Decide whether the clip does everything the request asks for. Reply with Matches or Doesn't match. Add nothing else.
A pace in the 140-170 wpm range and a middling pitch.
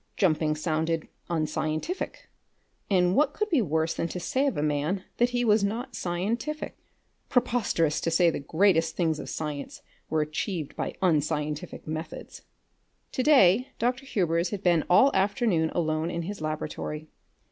Matches